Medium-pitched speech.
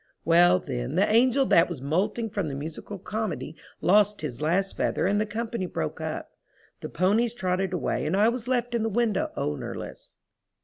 No: high, 195 Hz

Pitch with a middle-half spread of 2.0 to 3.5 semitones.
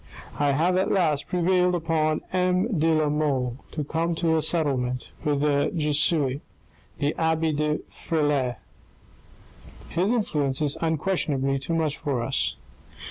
Yes: average, 2.7 semitones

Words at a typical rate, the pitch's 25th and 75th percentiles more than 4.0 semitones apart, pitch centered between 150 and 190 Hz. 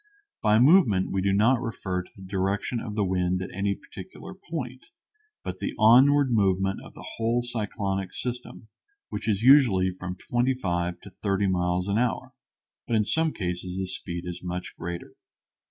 No: average, 170 wpm; average, 4.6 semitones; low, 100 Hz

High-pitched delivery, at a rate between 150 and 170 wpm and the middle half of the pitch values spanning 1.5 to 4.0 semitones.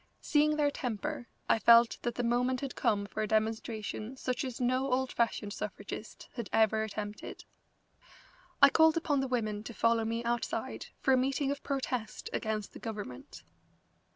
Yes: high, 235 Hz; average, 165 wpm; average, 3.3 semitones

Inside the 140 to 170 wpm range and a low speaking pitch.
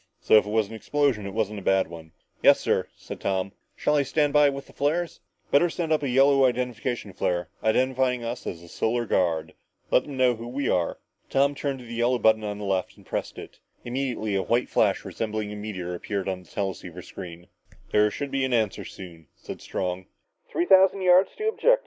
No: average, 200 wpm; low, 110 Hz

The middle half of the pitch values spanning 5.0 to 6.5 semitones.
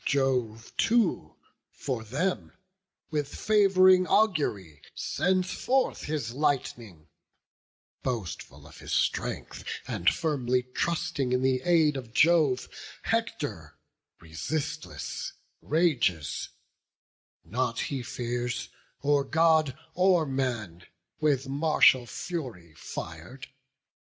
Yes: wide, 5.4 semitones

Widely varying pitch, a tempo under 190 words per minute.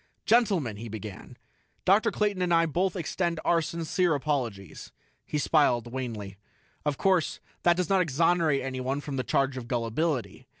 Yes: wide, 5.8 semitones; average, 155 wpm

